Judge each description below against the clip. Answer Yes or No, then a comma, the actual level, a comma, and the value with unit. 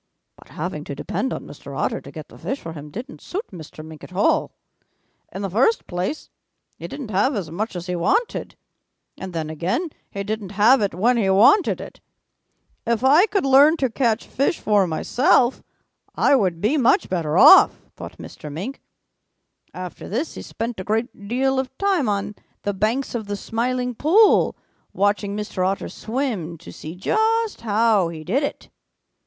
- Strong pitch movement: Yes, wide, 6.2 semitones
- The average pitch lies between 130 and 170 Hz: No, high, 215 Hz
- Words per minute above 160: Yes, average, 180 wpm